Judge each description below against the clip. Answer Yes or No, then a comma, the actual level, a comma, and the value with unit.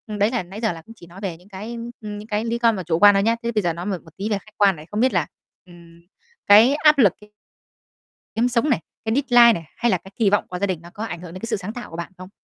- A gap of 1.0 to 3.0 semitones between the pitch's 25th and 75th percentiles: No, average, 4.1 semitones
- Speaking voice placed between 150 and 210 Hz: Yes, high, 205 Hz